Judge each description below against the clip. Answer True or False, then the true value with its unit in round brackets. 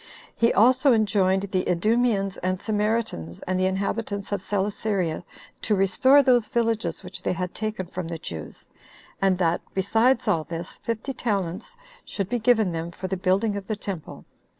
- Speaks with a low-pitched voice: False (200 Hz)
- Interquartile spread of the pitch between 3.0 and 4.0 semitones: True (3.3 semitones)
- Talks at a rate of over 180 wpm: False (165 wpm)